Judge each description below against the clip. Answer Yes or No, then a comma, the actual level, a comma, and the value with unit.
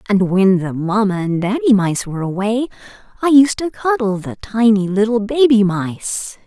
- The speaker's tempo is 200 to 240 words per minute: No, average, 165 wpm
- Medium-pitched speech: No, high, 210 Hz